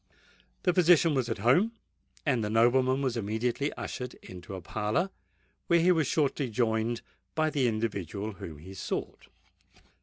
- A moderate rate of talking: Yes, average, 150 wpm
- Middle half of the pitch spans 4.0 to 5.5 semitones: Yes, average, 5.2 semitones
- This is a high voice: No, low, 120 Hz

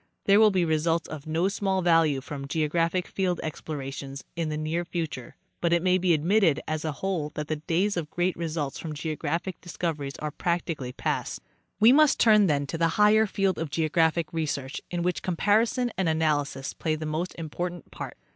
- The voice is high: No, medium, 165 Hz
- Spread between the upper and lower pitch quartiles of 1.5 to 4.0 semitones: Yes, average, 3.0 semitones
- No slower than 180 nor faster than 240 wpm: Yes, average, 185 wpm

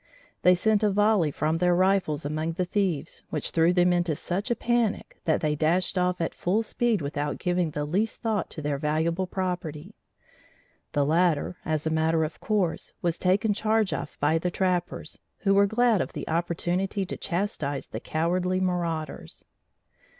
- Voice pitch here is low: No, medium, 180 Hz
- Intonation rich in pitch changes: No, average, 3.6 semitones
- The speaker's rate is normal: Yes, average, 170 wpm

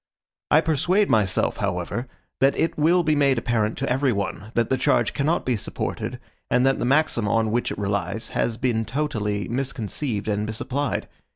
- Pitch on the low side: Yes, low, 120 Hz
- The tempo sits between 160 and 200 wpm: Yes, average, 175 wpm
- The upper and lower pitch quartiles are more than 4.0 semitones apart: Yes, average, 4.8 semitones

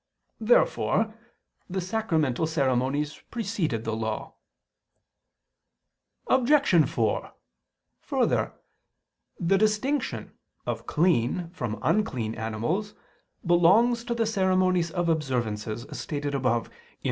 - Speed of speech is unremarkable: No, slow, 95 wpm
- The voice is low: No, medium, 170 Hz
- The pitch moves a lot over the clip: Yes, wide, 8.9 semitones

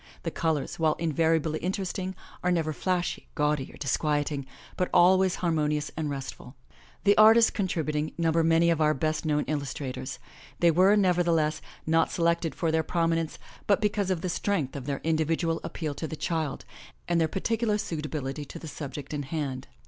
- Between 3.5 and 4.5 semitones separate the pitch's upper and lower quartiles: No, average, 2.7 semitones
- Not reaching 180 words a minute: Yes, average, 170 wpm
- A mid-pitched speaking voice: Yes, medium, 160 Hz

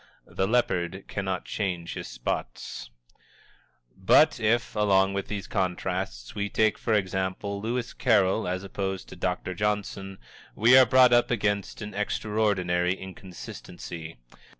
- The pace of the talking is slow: Yes, slow, 125 wpm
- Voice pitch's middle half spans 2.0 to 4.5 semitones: Yes, narrow, 2.5 semitones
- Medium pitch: No, low, 100 Hz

